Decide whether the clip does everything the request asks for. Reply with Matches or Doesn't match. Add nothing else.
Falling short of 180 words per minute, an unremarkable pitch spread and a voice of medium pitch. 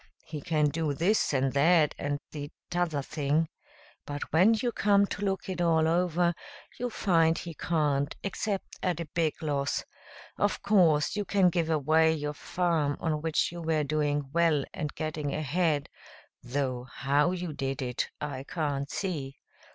Matches